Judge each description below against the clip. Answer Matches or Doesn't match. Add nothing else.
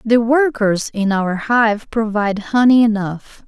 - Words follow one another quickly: Doesn't match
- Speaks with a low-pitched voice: Doesn't match